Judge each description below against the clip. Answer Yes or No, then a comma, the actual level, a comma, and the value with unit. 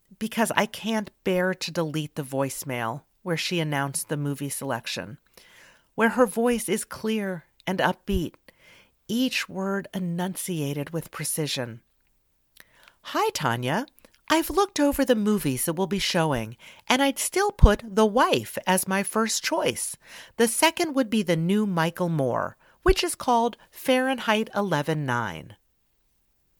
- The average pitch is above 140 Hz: Yes, high, 190 Hz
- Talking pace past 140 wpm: No, slow, 135 wpm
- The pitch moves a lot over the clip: Yes, wide, 7.4 semitones